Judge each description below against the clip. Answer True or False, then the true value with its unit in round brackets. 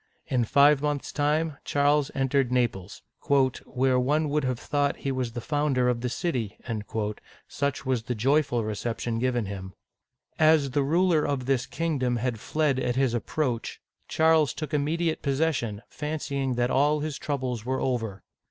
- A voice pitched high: False (135 Hz)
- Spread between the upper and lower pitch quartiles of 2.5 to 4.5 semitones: True (3.3 semitones)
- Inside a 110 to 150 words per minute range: False (160 wpm)